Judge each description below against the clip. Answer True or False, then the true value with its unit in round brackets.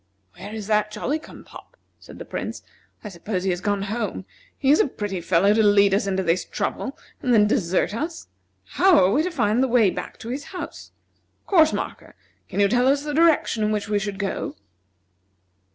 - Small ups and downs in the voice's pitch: False (5.4 semitones)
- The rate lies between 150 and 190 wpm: False (205 wpm)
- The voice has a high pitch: True (215 Hz)